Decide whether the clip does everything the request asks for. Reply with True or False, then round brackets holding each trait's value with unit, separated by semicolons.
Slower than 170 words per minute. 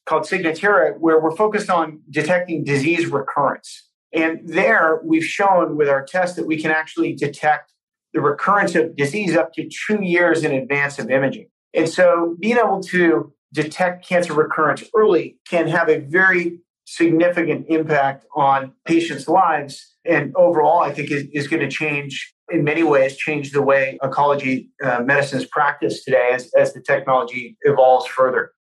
True (160 wpm)